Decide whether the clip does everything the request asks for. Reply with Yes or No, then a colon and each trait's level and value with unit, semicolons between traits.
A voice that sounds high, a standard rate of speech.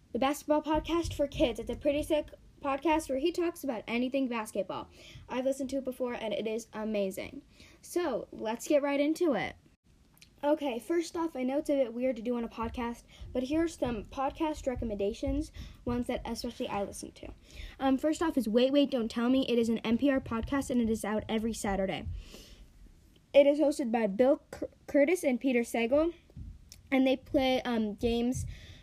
Yes: very high, 260 Hz; average, 190 wpm